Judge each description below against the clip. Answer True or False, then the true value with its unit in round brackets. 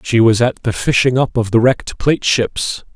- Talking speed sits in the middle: False (225 wpm)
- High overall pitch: False (120 Hz)